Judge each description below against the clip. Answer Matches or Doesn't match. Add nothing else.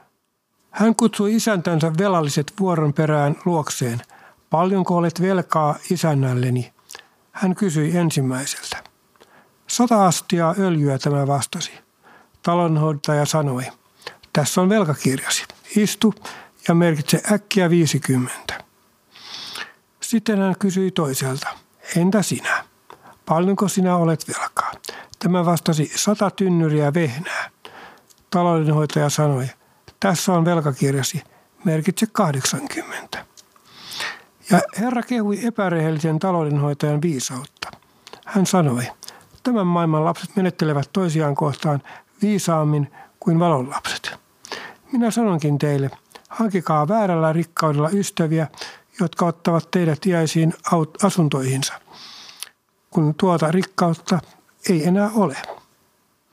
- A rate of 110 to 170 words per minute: Doesn't match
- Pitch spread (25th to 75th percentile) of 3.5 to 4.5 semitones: Matches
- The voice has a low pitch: Doesn't match